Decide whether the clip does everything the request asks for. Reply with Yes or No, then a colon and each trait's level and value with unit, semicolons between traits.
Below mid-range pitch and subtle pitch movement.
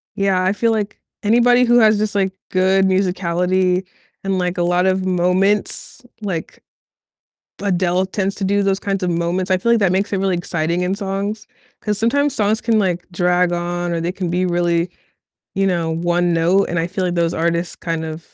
No: medium, 185 Hz; narrow, 2.2 semitones